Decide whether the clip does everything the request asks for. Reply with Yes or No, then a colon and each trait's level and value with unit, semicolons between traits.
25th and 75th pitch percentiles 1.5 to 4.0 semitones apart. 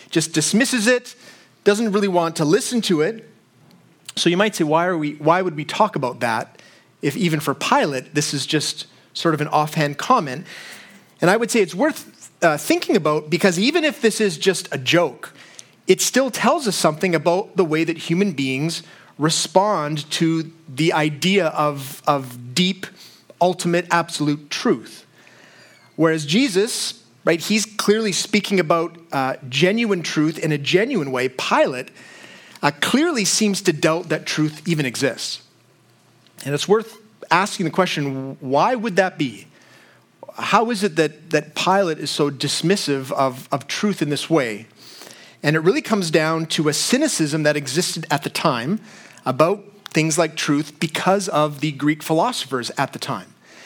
No: average, 5.1 semitones